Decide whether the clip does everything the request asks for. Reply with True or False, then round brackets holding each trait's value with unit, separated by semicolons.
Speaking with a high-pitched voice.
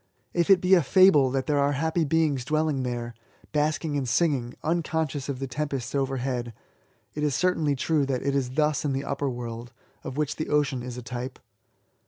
False (140 Hz)